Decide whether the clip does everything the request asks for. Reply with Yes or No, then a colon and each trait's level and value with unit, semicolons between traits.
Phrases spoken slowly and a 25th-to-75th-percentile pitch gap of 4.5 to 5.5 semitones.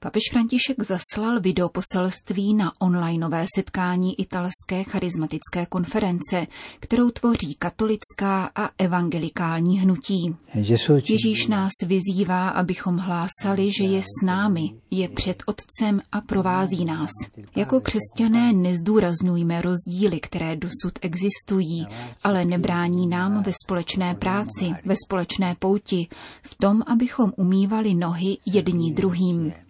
No: slow, 110 wpm; narrow, 2.4 semitones